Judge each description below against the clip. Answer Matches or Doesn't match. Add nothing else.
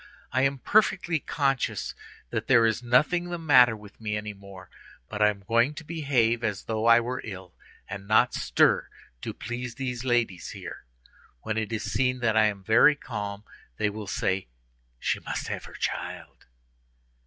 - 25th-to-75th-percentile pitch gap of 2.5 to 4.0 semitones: Matches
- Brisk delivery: Doesn't match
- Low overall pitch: Matches